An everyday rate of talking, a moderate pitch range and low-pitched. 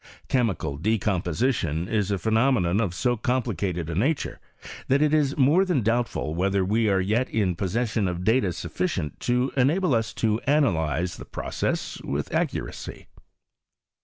No: average, 150 wpm; wide, 5.8 semitones; low, 110 Hz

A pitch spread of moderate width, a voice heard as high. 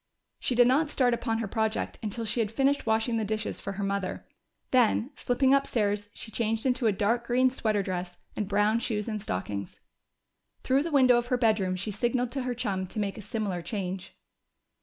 Yes: average, 3.4 semitones; high, 220 Hz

